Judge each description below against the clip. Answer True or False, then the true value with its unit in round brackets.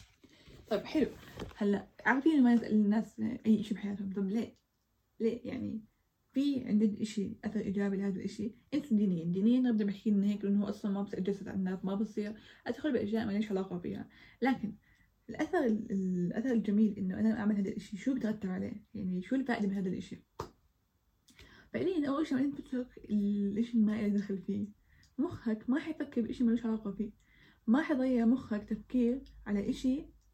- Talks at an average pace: False (165 wpm)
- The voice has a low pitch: False (215 Hz)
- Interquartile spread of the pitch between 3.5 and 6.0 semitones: False (3.1 semitones)